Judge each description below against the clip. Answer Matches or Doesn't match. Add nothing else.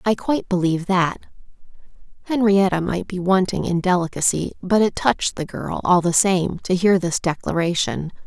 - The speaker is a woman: Matches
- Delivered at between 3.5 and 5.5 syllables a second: Matches